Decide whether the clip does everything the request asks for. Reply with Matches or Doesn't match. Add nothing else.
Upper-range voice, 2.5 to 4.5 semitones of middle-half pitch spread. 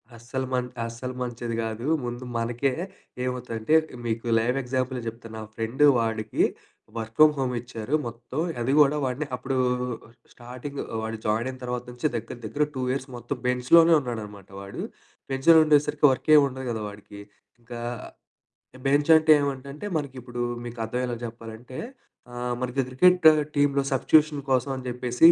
Doesn't match